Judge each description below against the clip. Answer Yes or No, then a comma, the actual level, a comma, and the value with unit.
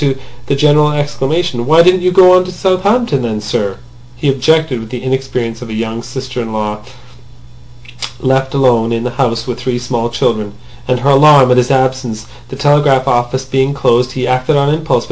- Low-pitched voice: Yes, low, 130 Hz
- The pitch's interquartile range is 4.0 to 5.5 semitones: No, average, 3.4 semitones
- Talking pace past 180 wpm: Yes, average, 190 wpm